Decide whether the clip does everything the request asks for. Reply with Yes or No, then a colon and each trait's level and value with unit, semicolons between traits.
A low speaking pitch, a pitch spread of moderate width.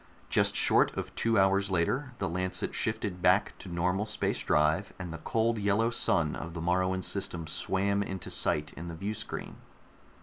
Yes: very low, 95 Hz; average, 3.0 semitones